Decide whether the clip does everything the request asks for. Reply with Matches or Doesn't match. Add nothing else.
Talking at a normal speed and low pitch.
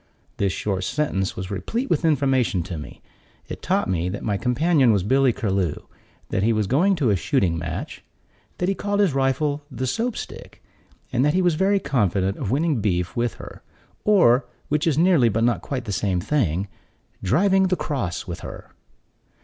Matches